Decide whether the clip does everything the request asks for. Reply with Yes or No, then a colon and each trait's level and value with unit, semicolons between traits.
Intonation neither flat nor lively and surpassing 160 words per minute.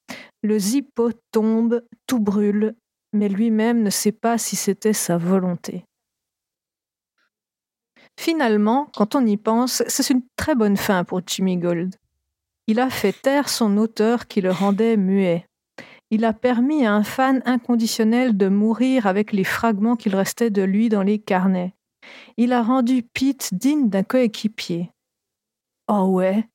No: average, 3.5 semitones; slow, 145 wpm